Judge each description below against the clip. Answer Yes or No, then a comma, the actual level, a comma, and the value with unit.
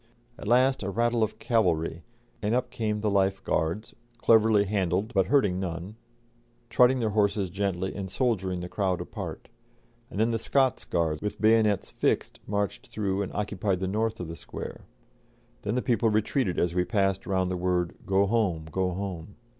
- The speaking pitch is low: Yes, low, 100 Hz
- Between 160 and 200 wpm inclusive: Yes, average, 175 wpm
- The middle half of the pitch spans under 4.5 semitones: Yes, average, 3.3 semitones